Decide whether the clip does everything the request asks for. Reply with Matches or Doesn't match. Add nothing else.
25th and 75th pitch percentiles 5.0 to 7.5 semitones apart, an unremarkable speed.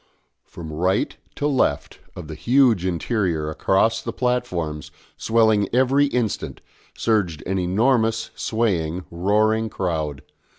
Doesn't match